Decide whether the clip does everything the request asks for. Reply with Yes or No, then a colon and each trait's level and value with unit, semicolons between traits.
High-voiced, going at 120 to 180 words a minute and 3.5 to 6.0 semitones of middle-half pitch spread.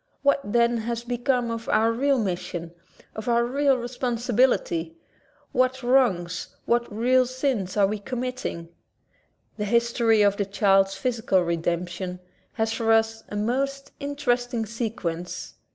Yes: high, 230 Hz; slow, 135 wpm; average, 3.8 semitones